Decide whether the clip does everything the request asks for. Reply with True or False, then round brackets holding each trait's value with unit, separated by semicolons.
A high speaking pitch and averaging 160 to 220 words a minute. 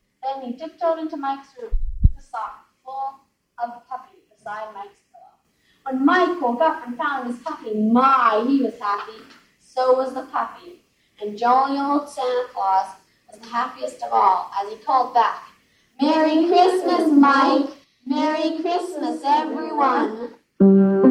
False (270 Hz; 150 wpm)